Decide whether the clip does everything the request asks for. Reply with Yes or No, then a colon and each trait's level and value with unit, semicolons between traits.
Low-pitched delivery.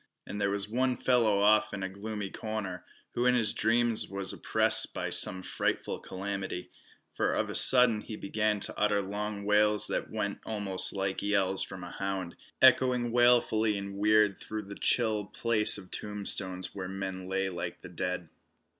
Yes: low, 105 Hz